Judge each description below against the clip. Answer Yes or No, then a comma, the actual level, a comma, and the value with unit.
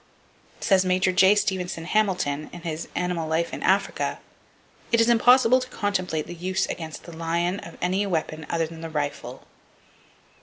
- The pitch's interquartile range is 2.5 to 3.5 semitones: Yes, average, 3.0 semitones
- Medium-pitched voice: Yes, medium, 180 Hz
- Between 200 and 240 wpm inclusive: No, average, 160 wpm